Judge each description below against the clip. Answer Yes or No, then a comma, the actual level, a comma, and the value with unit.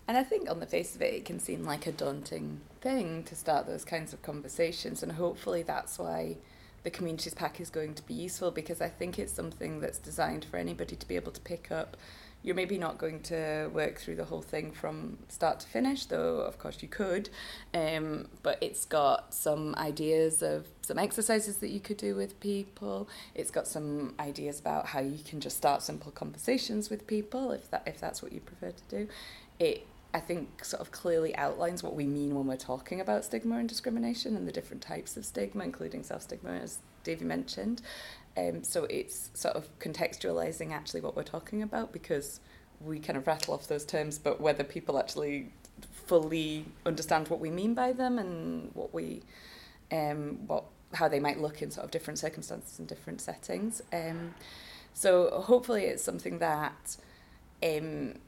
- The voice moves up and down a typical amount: No, wide, 6.1 semitones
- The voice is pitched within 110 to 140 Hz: No, medium, 165 Hz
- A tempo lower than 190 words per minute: No, average, 195 wpm